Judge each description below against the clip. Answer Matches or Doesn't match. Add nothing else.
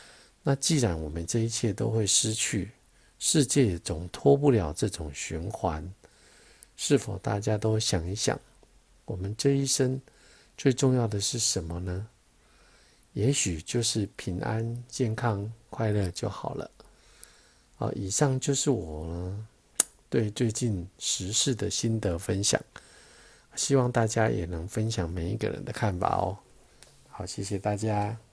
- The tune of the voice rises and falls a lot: Doesn't match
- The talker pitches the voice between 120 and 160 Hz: Doesn't match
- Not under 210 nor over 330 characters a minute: Doesn't match